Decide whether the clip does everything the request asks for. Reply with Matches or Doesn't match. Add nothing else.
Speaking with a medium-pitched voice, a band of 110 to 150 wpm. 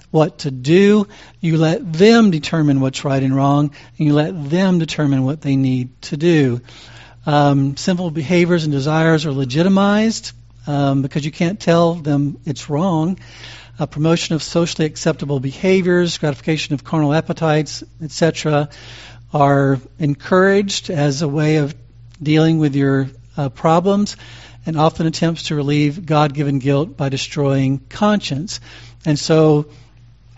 Matches